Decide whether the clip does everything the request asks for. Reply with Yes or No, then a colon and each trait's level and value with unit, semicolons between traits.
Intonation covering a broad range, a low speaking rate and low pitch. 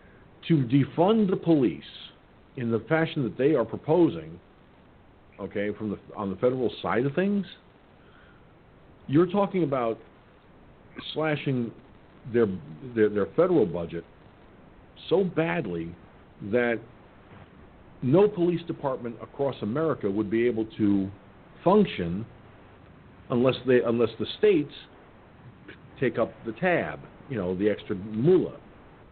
Yes: wide, 7.3 semitones; slow, 115 wpm; low, 120 Hz